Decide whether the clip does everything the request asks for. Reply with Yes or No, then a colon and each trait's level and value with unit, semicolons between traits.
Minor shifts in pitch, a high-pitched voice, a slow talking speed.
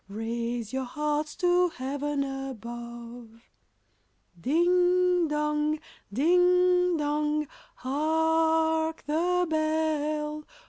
No: average, 3.2 semitones; very high, 300 Hz; slow, 80 wpm